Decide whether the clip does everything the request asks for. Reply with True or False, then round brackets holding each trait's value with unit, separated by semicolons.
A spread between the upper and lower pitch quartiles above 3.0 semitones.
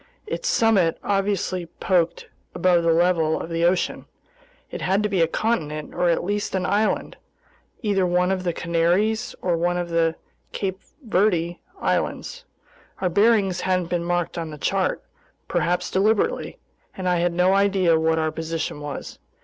False (2.7 semitones)